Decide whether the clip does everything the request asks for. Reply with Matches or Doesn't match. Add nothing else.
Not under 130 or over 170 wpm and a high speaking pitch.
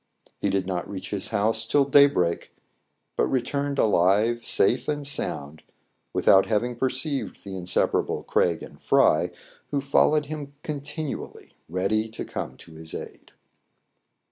Doesn't match